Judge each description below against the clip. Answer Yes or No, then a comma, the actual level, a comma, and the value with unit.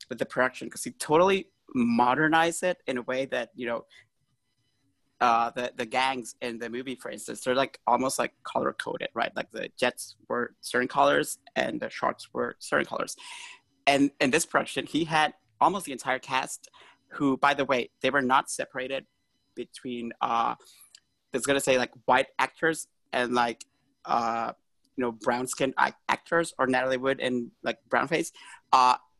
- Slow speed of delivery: No, average, 175 wpm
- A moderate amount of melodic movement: No, narrow, 2.2 semitones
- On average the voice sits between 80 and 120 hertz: No, low, 130 Hz